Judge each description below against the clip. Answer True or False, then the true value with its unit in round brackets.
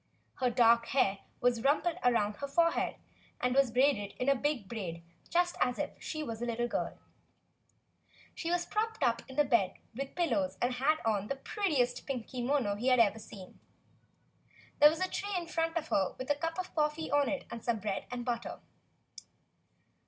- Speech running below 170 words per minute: False (195 wpm)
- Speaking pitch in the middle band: False (255 Hz)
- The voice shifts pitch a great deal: False (4.8 semitones)